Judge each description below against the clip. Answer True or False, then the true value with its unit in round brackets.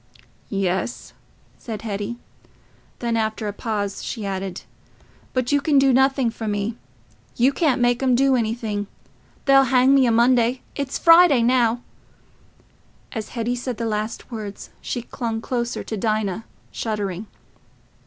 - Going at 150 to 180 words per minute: False (135 wpm)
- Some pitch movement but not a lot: True (3.1 semitones)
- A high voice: True (235 Hz)